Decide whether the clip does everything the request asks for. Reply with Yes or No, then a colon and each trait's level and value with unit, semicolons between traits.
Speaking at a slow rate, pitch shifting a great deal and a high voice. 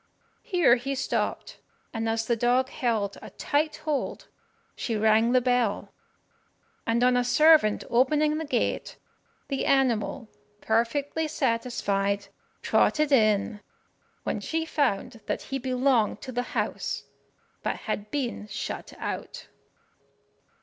No: slow, 120 wpm; average, 3.6 semitones; high, 245 Hz